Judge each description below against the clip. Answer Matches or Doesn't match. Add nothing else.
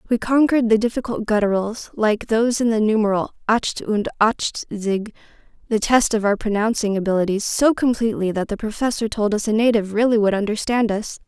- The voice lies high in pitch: Matches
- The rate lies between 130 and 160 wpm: Doesn't match